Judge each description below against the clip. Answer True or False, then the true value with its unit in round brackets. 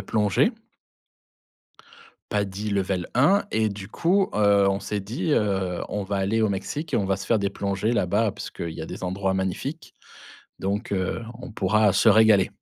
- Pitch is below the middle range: True (100 Hz)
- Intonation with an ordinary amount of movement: False (2.3 semitones)